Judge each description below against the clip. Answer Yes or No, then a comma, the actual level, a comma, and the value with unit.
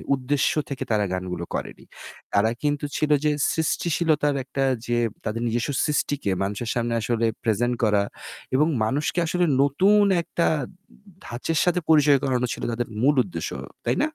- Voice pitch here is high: No, low, 135 Hz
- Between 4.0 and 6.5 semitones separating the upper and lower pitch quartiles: Yes, average, 4.7 semitones